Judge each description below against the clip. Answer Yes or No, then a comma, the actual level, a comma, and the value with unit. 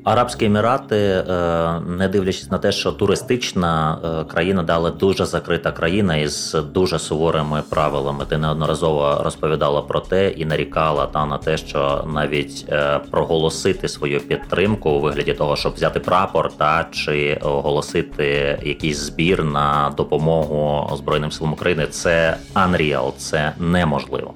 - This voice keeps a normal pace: Yes, average, 130 wpm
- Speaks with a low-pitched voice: Yes, very low, 80 Hz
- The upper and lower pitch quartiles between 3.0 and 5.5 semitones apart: No, narrow, 2.6 semitones